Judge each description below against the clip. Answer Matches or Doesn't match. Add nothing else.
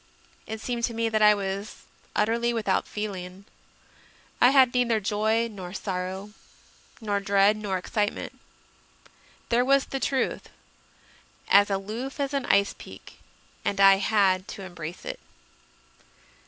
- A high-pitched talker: Matches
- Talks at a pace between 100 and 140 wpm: Matches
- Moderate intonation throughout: Matches